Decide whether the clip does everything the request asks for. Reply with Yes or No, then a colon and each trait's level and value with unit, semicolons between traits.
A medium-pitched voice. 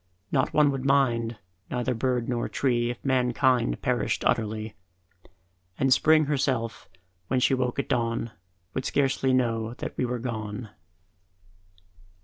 No: low, 125 Hz